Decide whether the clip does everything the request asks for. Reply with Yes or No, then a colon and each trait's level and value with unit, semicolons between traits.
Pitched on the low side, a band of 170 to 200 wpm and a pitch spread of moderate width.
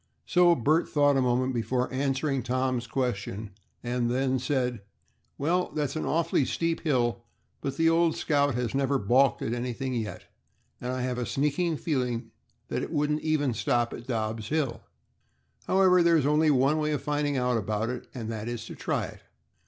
Yes: low, 130 Hz; average, 180 wpm; average, 3.7 semitones